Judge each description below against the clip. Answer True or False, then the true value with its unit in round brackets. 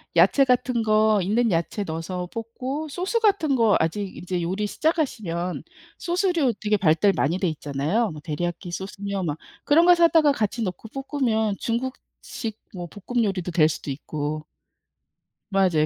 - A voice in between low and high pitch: False (205 Hz)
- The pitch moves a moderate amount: False (6.4 semitones)